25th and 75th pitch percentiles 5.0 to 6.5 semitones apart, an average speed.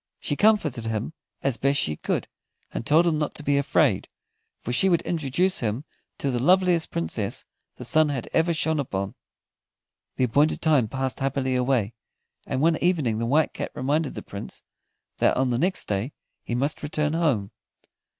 No: average, 4.6 semitones; average, 175 wpm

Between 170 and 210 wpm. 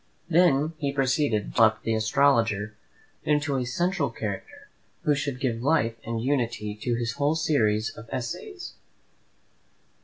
No: average, 140 wpm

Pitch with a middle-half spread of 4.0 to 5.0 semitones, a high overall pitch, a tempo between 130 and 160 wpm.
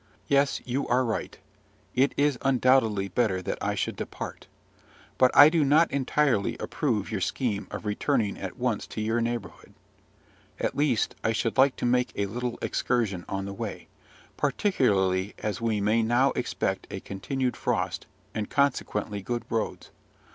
No: average, 4.4 semitones; low, 120 Hz; average, 155 wpm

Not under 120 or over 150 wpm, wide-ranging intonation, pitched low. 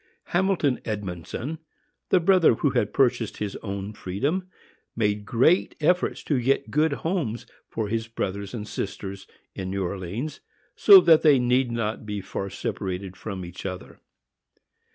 Yes: average, 145 wpm; wide, 7.1 semitones; low, 115 Hz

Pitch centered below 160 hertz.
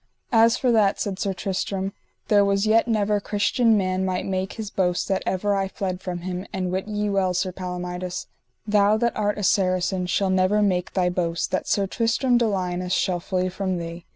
No: high, 190 Hz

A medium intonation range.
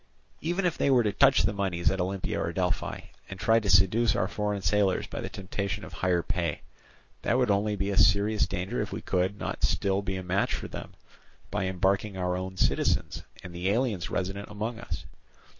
No: narrow, 2.1 semitones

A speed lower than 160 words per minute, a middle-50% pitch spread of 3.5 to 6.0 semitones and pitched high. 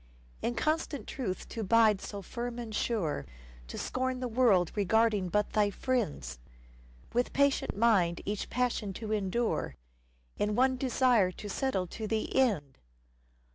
Yes: average, 140 wpm; average, 4.2 semitones; high, 220 Hz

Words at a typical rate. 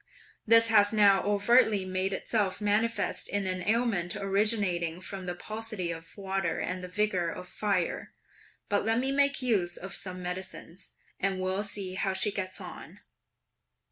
Yes: average, 155 wpm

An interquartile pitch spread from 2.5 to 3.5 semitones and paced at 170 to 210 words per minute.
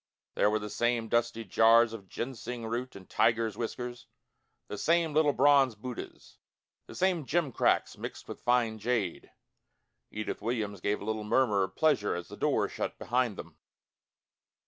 No: average, 3.1 semitones; average, 160 wpm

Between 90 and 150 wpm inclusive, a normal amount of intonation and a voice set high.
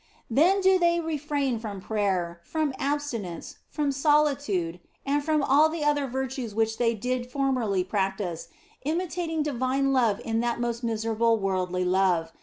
No: average, 145 wpm; wide, 6.2 semitones; high, 245 Hz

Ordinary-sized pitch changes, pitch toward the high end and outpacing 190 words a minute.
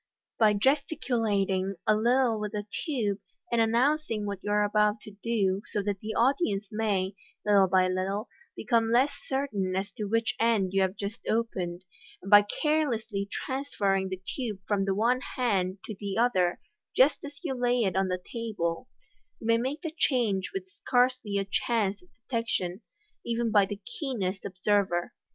No: average, 3.6 semitones; high, 210 Hz; average, 175 wpm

